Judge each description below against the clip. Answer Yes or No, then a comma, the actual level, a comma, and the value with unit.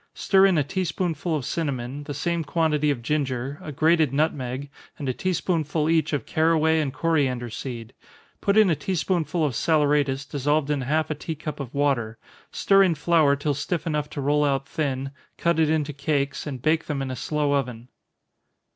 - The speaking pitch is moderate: Yes, medium, 150 Hz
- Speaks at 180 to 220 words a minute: Yes, average, 195 wpm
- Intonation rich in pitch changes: No, narrow, 2.6 semitones